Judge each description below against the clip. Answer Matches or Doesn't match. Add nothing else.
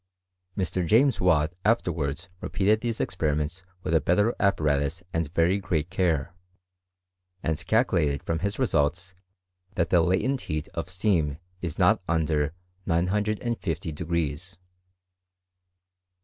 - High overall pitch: Doesn't match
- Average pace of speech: Doesn't match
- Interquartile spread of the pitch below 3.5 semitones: Doesn't match